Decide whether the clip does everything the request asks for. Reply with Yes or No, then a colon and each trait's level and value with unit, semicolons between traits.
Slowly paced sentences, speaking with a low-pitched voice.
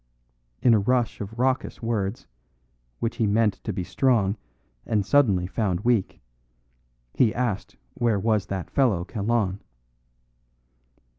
Yes: slow, 125 wpm; low, 110 Hz